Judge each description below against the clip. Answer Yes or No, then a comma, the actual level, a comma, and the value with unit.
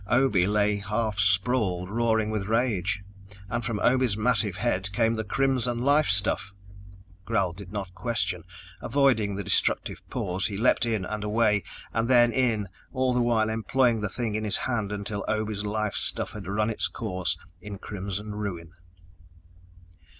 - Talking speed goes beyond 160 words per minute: No, average, 155 wpm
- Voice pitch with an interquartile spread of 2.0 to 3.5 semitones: Yes, average, 2.8 semitones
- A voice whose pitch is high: No, low, 105 Hz